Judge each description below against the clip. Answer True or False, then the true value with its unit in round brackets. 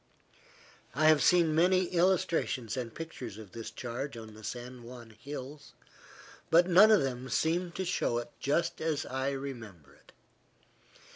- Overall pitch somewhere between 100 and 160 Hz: True (135 Hz)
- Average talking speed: True (150 wpm)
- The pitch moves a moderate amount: False (5.9 semitones)